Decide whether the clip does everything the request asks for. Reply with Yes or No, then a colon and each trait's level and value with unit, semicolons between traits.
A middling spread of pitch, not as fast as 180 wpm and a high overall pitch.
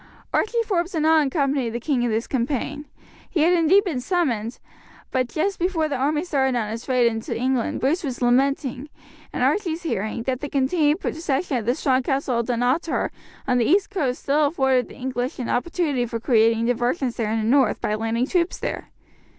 No: average, 4.5 semitones; average, 190 wpm; very high, 265 Hz